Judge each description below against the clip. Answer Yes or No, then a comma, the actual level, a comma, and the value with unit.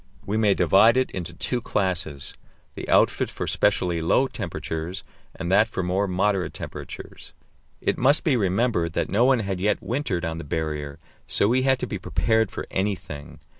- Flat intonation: No, average, 4.8 semitones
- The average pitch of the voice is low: Yes, very low, 95 Hz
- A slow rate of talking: No, average, 175 wpm